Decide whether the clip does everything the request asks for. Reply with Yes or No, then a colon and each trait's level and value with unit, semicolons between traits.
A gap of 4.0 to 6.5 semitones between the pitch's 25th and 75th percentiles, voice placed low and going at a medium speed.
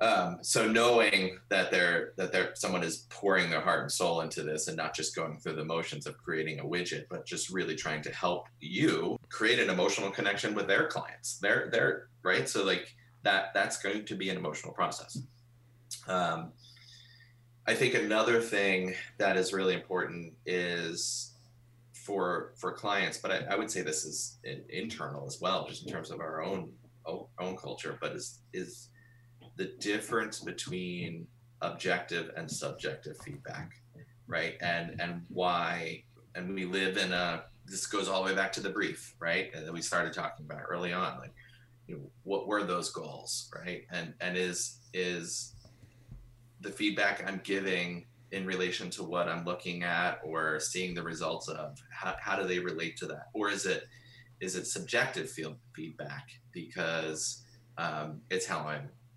Yes: wide, 5.4 semitones; low, 100 Hz; average, 175 wpm